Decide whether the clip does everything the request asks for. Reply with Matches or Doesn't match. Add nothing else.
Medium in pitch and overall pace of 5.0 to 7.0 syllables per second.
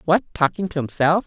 Matches